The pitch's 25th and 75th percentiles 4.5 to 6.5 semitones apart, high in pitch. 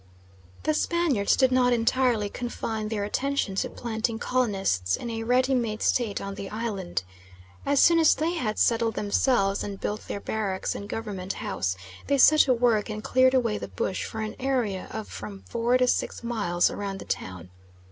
No: average, 3.9 semitones; high, 225 Hz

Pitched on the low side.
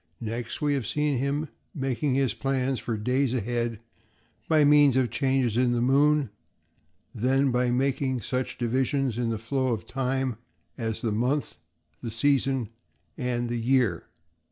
Yes: low, 130 Hz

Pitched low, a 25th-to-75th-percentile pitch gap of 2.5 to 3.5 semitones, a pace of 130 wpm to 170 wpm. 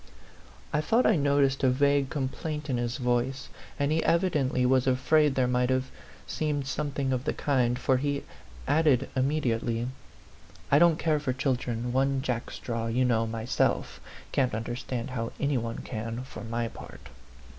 Yes: low, 130 Hz; average, 2.8 semitones; average, 155 wpm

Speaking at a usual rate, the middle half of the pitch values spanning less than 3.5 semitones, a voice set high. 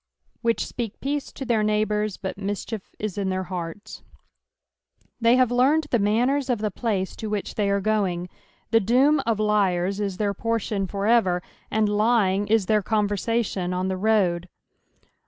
Yes: average, 170 wpm; average, 3.0 semitones; high, 210 Hz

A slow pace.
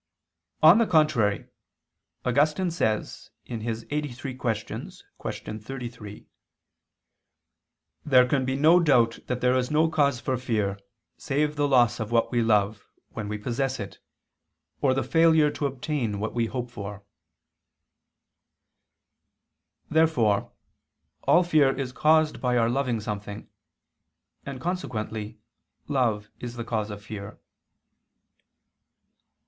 Yes: slow, 120 wpm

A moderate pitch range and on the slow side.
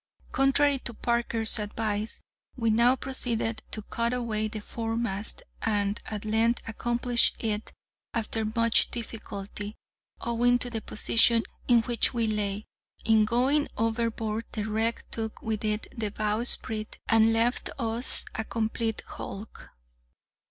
No: narrow, 1.6 semitones; slow, 130 wpm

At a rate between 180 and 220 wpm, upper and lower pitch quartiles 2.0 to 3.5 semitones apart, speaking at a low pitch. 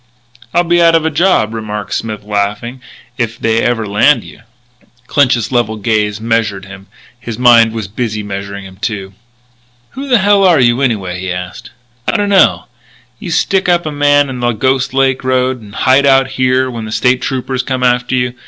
No: average, 190 wpm; average, 4.0 semitones; low, 120 Hz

